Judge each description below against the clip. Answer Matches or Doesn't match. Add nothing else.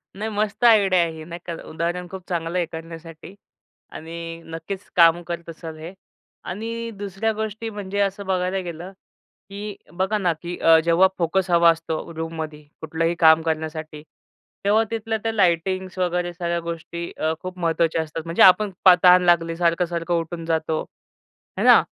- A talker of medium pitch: Matches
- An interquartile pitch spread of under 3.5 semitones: Matches